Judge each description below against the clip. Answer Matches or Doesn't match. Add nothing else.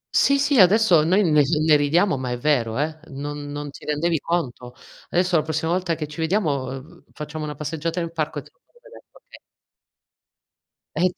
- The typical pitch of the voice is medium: Matches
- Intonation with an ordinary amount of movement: Matches